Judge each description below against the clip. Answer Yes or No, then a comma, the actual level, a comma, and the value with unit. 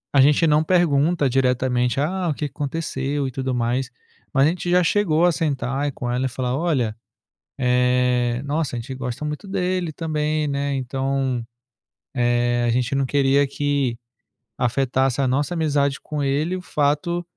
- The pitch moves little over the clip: No, average, 3.3 semitones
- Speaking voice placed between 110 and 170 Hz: Yes, medium, 140 Hz